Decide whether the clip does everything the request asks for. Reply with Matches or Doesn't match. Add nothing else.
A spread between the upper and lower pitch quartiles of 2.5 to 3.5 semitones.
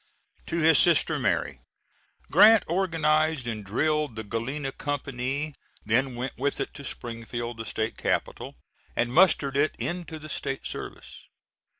Doesn't match